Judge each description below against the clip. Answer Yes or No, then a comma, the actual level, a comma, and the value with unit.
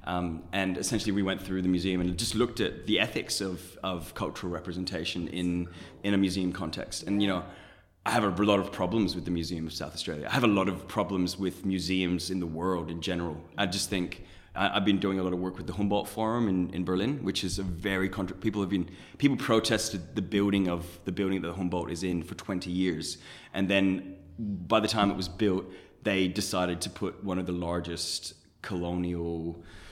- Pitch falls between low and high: No, very low, 95 Hz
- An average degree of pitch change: No, narrow, 2.2 semitones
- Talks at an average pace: No, fast, 215 wpm